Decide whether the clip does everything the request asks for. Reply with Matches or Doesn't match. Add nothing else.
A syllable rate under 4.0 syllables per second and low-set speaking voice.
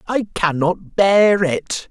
Doesn't match